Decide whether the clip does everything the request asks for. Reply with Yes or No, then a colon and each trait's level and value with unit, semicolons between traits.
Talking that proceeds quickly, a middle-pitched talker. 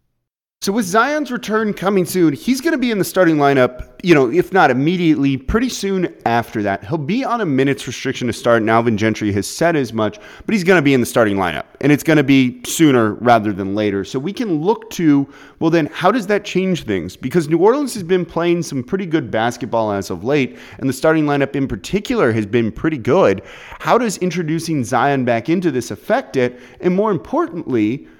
Yes: fast, 220 wpm; medium, 145 Hz